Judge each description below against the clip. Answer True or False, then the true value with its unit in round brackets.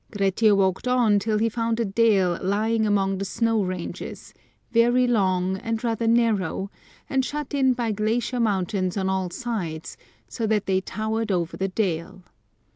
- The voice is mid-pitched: False (210 Hz)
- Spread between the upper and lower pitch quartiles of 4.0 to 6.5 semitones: False (3.2 semitones)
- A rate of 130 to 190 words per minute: True (160 wpm)